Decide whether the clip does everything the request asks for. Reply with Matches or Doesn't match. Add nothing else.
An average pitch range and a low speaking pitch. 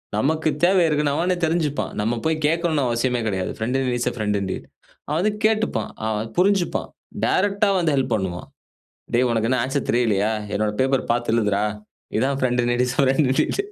Doesn't match